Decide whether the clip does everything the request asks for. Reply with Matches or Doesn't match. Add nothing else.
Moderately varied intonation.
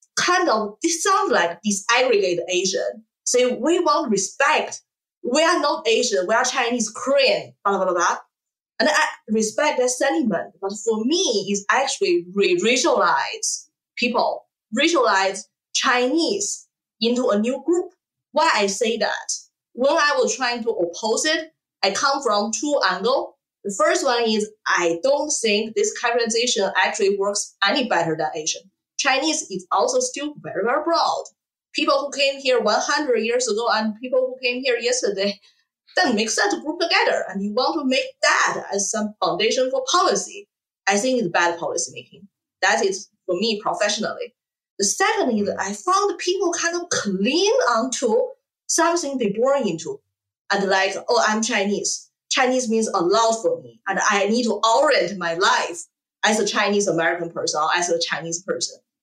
Doesn't match